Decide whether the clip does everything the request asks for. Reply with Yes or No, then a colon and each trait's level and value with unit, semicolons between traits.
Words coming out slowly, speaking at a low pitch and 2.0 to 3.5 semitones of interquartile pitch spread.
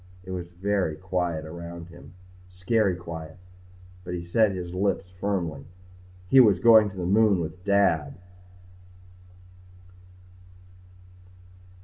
Yes: slow, 110 wpm; very low, 90 Hz; narrow, 2.6 semitones